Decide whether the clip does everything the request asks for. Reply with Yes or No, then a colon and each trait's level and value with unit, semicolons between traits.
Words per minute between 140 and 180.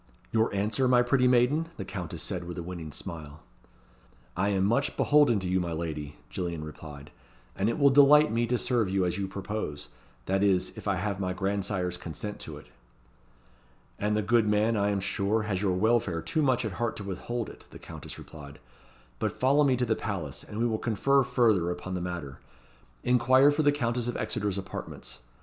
No: average, 200 wpm